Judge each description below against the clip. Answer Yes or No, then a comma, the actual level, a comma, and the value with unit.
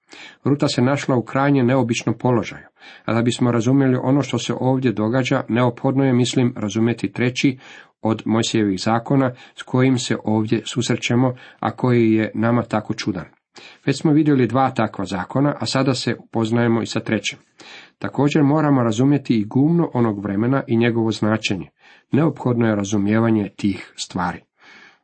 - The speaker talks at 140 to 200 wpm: Yes, average, 150 wpm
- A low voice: Yes, low, 120 Hz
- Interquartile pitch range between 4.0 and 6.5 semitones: No, average, 3.2 semitones